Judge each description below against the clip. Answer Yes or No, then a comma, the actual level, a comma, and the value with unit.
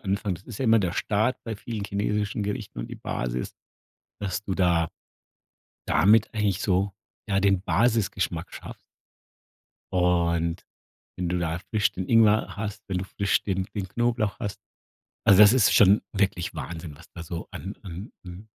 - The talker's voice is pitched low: Yes, low, 100 Hz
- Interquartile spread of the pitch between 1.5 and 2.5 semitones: No, average, 2.9 semitones